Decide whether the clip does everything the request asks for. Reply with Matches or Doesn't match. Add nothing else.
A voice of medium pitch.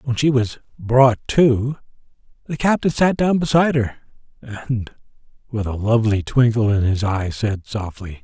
Doesn't match